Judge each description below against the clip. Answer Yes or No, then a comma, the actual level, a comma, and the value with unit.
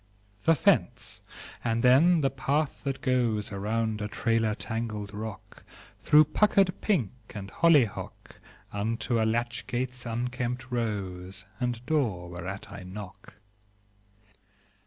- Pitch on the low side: Yes, low, 115 Hz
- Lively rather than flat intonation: No, average, 3.8 semitones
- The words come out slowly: Yes, slow, 115 wpm